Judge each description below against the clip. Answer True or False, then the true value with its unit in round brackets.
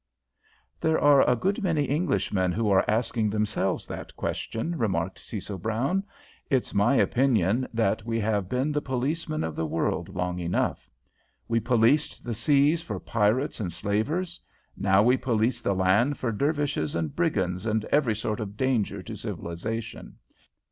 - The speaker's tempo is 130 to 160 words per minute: True (155 wpm)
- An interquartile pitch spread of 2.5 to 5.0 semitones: False (5.5 semitones)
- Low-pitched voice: True (115 Hz)